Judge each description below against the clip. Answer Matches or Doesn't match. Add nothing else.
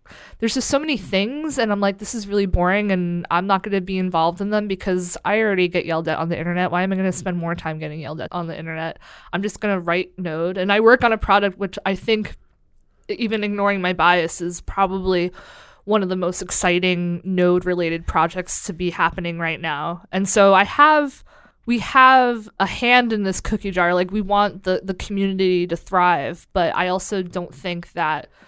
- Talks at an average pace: Doesn't match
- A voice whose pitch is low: Doesn't match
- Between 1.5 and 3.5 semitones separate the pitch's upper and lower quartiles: Matches